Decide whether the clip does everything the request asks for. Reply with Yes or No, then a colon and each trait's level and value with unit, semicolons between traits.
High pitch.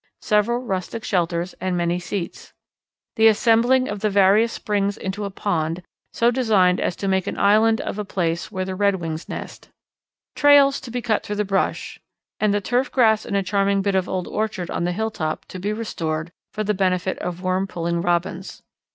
Yes: high, 195 Hz